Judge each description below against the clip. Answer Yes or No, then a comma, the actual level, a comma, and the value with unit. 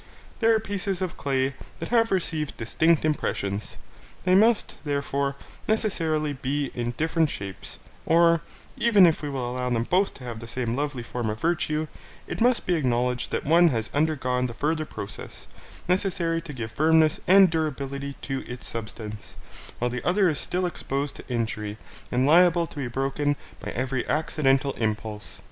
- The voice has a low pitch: No, medium, 145 Hz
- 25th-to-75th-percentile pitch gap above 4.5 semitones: Yes, average, 5.2 semitones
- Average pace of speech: Yes, average, 165 wpm